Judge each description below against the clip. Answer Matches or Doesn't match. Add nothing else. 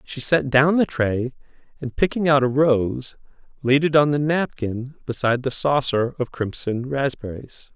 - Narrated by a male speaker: Matches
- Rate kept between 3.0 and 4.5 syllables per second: Matches